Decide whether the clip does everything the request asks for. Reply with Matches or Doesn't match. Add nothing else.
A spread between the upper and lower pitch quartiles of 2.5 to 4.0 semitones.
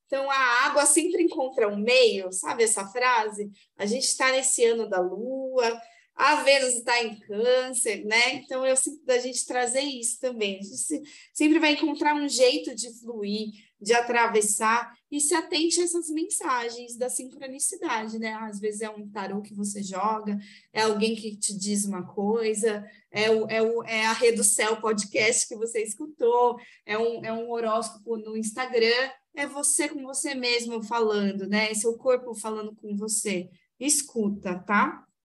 Matches